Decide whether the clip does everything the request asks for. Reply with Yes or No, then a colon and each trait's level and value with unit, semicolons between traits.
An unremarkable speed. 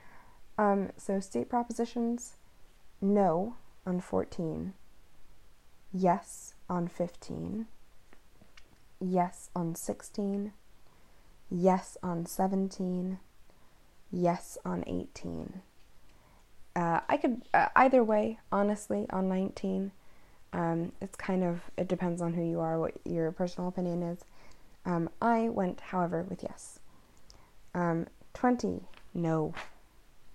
No: slow, 105 wpm